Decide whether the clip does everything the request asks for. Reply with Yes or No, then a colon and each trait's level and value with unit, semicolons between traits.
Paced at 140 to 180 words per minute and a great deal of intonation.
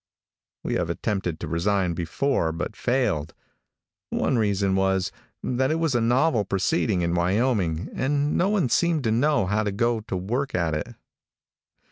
Yes: average, 160 wpm; wide, 6.5 semitones